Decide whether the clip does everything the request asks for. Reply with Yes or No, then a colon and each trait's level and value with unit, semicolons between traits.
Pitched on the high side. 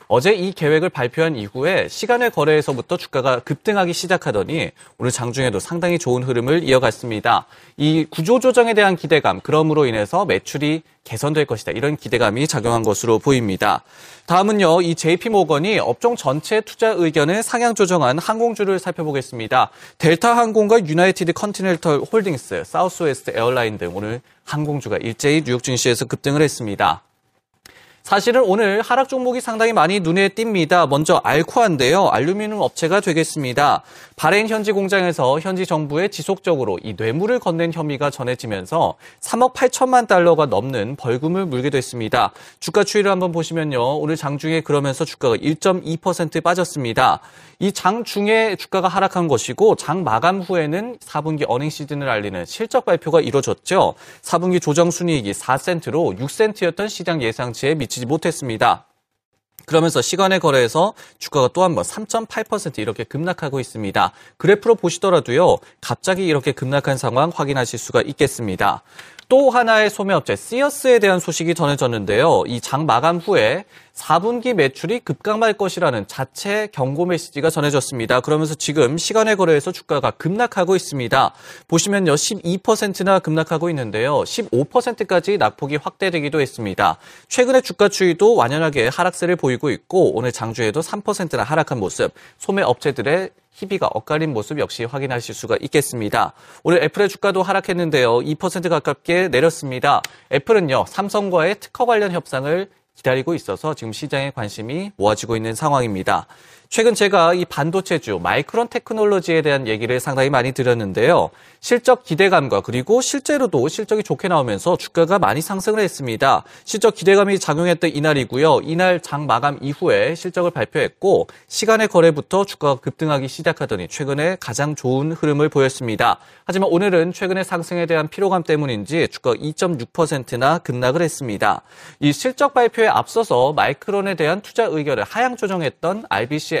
No: medium, 165 Hz